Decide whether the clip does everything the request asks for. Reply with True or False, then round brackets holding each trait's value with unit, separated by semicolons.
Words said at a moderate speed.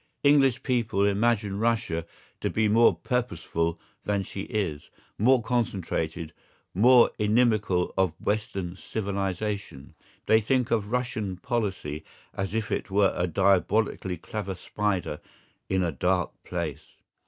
False (120 wpm)